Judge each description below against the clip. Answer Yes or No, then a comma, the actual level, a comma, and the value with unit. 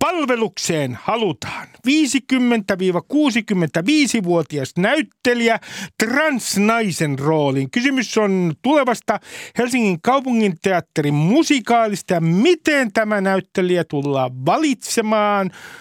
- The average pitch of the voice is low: No, high, 215 Hz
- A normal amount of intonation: No, wide, 6.5 semitones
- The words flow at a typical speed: No, slow, 70 wpm